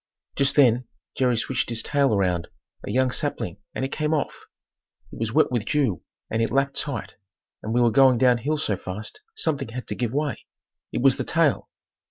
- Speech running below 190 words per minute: No, average, 200 wpm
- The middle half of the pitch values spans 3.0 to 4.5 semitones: Yes, average, 3.5 semitones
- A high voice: No, low, 125 Hz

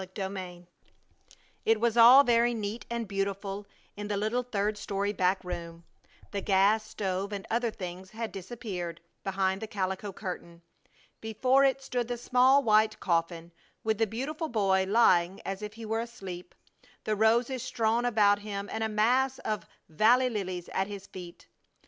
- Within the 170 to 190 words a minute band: No, average, 160 wpm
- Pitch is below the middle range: No, high, 210 Hz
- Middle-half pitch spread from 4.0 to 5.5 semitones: No, average, 3.4 semitones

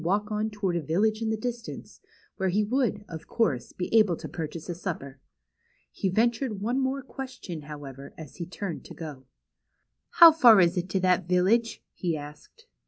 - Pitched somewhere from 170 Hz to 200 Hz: Yes, high, 190 Hz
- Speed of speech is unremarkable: Yes, average, 180 wpm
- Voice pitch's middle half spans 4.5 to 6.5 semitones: Yes, average, 5.3 semitones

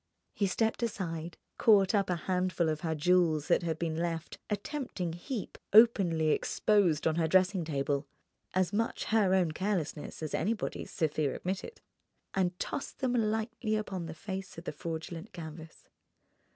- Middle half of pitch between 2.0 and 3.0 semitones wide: No, average, 4.2 semitones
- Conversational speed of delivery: Yes, average, 155 wpm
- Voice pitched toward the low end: No, medium, 180 Hz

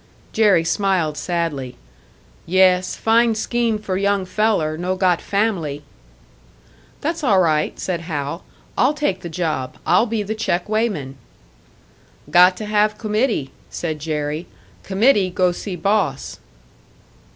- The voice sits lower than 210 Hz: Yes, medium, 185 Hz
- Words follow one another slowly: Yes, slow, 125 wpm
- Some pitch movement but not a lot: Yes, average, 4.6 semitones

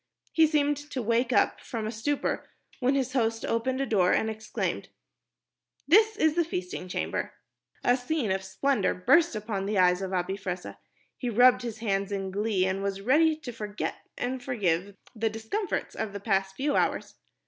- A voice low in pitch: No, high, 225 Hz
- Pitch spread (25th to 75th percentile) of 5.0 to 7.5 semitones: Yes, wide, 5.4 semitones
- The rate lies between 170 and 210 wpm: Yes, average, 180 wpm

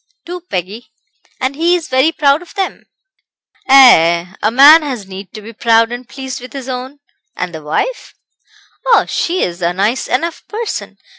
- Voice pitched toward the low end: No, very high, 255 Hz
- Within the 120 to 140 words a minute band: No, average, 170 wpm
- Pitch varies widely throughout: Yes, wide, 7.1 semitones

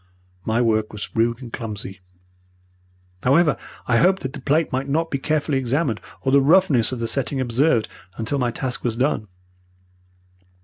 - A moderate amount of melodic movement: Yes, average, 3.8 semitones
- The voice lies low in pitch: Yes, low, 130 Hz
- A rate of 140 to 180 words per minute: Yes, average, 165 wpm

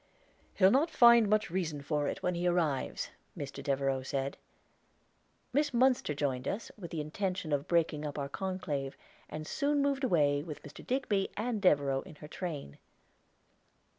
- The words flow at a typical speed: Yes, average, 160 wpm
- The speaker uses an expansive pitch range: Yes, wide, 6.4 semitones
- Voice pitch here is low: No, medium, 165 Hz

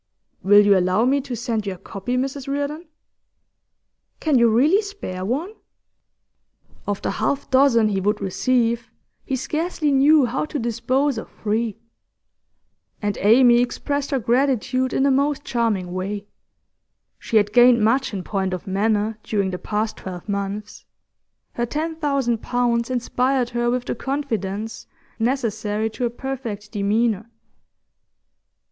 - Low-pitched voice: No, high, 235 Hz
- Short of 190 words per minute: Yes, average, 140 wpm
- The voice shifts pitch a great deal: No, average, 4.4 semitones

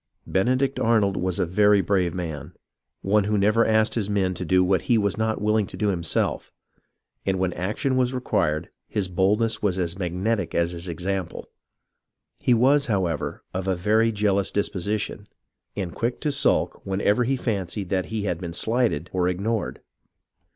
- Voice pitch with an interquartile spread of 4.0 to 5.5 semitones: No, average, 3.3 semitones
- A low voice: Yes, low, 100 Hz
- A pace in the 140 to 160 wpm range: No, average, 170 wpm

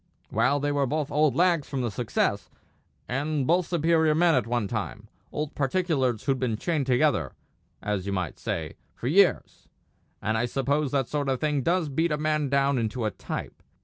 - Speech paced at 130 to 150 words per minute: No, average, 185 wpm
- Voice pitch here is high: No, medium, 140 Hz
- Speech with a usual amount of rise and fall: Yes, average, 4.1 semitones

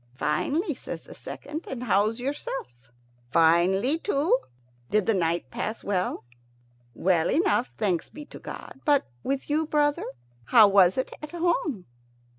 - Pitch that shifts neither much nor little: No, wide, 7.9 semitones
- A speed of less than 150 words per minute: Yes, average, 140 wpm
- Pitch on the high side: Yes, high, 245 Hz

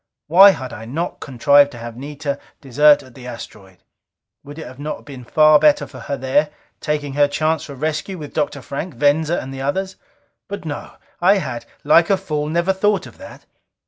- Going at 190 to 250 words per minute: Yes, average, 195 wpm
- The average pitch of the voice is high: No, medium, 145 Hz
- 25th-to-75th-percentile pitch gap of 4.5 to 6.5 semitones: No, average, 3.1 semitones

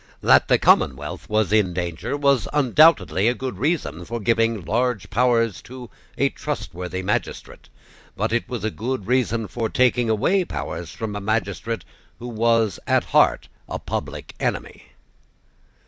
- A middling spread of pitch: Yes, average, 3.6 semitones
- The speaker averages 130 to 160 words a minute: Yes, average, 145 wpm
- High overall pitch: No, low, 115 Hz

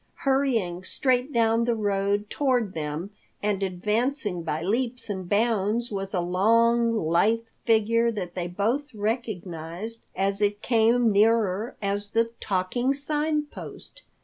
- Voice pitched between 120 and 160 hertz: No, high, 215 Hz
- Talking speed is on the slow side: Yes, slow, 130 wpm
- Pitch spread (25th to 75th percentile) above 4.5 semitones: No, average, 3.5 semitones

